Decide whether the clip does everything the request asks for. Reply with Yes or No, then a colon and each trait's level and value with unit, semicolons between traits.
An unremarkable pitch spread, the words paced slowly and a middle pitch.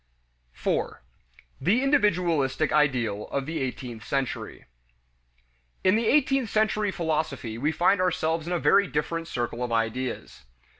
No: wide, 6.7 semitones; slow, 130 wpm; medium, 160 Hz